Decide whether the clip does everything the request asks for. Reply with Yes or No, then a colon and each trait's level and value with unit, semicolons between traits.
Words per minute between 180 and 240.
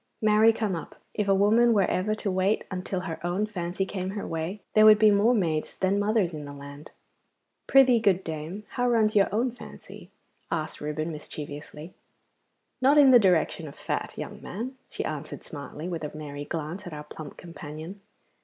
Yes: average, 185 wpm